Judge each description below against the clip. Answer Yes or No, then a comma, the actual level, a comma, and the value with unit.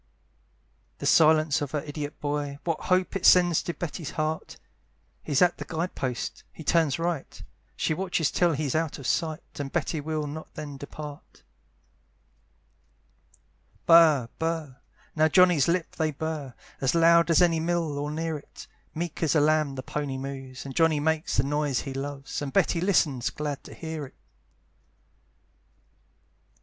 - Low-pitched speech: No, medium, 155 Hz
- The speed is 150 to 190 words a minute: Yes, average, 160 wpm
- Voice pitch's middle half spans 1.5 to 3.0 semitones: Yes, narrow, 2.6 semitones